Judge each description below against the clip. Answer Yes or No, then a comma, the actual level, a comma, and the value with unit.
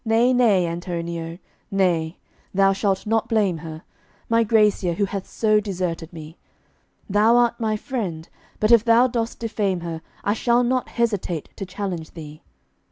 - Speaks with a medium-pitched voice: No, high, 200 Hz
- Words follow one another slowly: No, average, 155 wpm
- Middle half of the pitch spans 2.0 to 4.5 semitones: No, average, 4.9 semitones